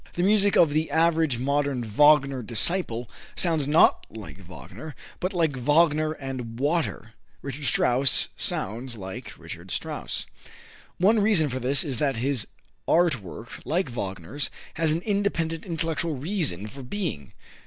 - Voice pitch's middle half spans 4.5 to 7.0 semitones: Yes, average, 5.3 semitones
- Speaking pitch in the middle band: Yes, medium, 145 Hz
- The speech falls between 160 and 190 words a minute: No, average, 140 wpm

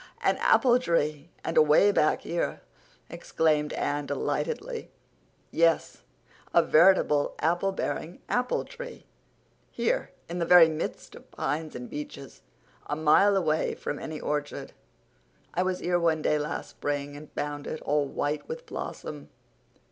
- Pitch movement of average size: Yes, average, 3.5 semitones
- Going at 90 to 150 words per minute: Yes, average, 140 wpm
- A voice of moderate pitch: Yes, medium, 155 Hz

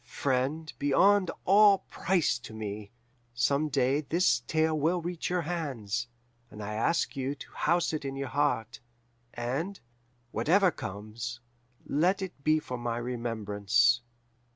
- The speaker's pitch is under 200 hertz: Yes, medium, 140 Hz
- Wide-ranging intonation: Yes, wide, 5.7 semitones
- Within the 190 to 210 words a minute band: No, slow, 135 wpm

